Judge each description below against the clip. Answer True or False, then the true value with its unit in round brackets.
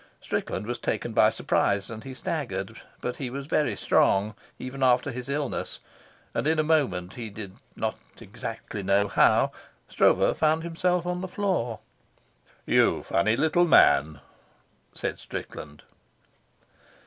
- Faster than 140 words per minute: False (135 wpm)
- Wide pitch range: True (7.5 semitones)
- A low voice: True (125 Hz)